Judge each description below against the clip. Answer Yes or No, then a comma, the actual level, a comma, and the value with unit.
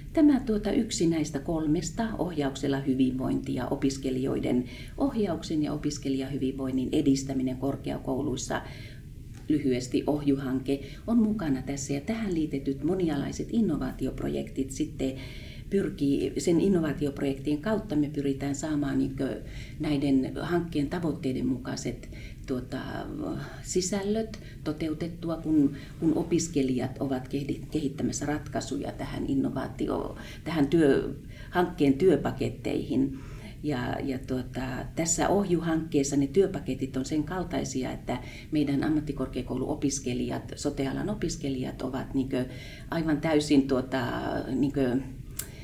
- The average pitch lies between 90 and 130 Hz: No, medium, 140 Hz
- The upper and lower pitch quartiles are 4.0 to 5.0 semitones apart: No, average, 2.9 semitones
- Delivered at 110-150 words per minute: No, slow, 95 wpm